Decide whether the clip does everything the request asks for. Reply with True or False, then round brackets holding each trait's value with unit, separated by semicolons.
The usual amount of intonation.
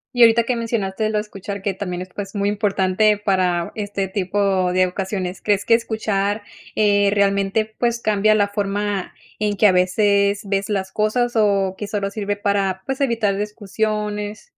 False (1.6 semitones)